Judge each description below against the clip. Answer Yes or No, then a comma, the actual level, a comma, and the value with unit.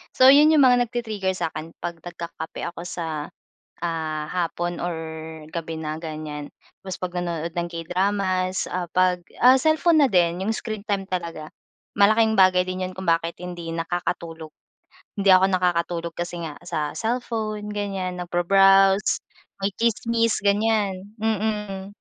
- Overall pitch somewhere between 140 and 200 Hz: Yes, medium, 185 Hz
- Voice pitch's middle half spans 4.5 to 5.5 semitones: No, average, 3.6 semitones